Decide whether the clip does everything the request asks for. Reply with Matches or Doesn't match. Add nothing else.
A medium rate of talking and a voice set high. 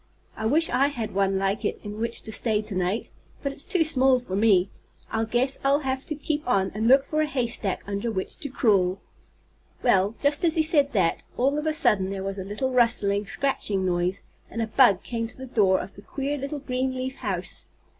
Doesn't match